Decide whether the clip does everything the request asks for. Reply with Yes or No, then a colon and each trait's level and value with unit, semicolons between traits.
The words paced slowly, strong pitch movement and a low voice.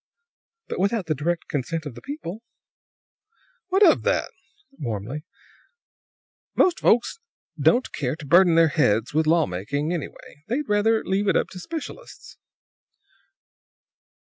No: slow, 130 wpm; wide, 7.2 semitones; medium, 170 Hz